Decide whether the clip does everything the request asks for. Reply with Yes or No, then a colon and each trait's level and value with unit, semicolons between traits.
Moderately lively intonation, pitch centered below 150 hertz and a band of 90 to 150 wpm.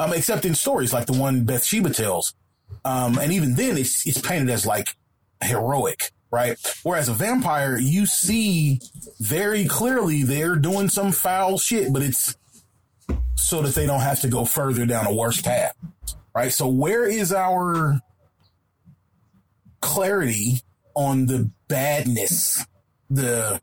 No: wide, 6.3 semitones; low, 135 Hz; average, 140 wpm